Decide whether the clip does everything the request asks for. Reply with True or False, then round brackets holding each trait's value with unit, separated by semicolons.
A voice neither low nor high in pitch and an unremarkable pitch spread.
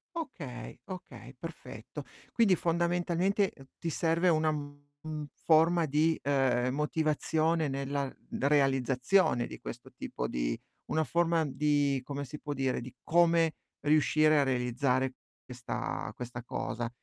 True (145 Hz; 3.7 semitones)